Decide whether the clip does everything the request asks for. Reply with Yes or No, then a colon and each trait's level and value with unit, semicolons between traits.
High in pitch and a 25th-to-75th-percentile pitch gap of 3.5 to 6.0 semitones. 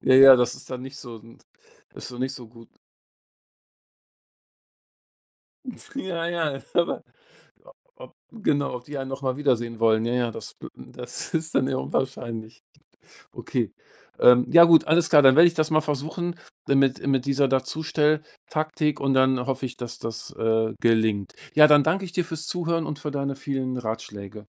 No: low, 135 Hz; average, 4.1 semitones